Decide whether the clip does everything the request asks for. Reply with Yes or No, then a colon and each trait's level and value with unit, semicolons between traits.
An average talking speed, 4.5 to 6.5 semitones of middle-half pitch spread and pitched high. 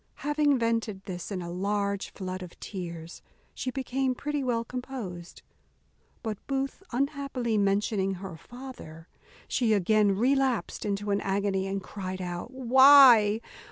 No: slow, 130 wpm; average, 5.1 semitones; high, 210 Hz